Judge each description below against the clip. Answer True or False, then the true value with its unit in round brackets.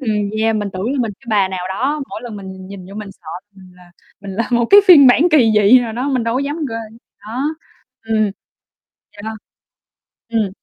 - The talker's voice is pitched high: True (220 Hz)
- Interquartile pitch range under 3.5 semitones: False (4.0 semitones)